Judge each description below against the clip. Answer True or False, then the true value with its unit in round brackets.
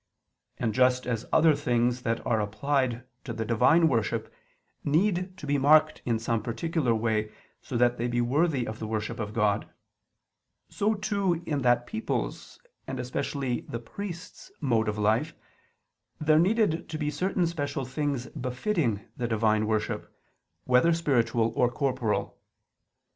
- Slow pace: False (150 wpm)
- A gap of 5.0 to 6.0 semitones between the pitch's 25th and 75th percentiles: True (5.3 semitones)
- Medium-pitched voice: False (125 Hz)